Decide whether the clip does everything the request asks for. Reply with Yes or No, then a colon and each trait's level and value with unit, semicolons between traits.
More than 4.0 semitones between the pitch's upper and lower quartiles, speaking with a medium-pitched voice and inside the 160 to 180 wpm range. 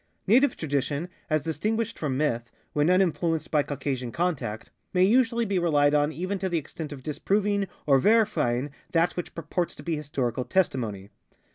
Yes: average, 5.0 semitones; medium, 160 Hz; average, 165 wpm